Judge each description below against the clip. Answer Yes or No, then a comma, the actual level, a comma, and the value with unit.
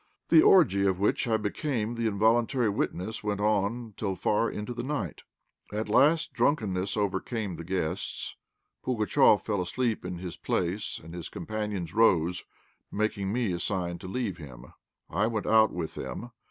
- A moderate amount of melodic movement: Yes, average, 3.7 semitones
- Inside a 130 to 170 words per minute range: Yes, average, 160 wpm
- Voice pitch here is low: Yes, low, 105 Hz